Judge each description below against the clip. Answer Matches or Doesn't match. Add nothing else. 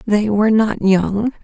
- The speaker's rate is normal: Matches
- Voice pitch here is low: Doesn't match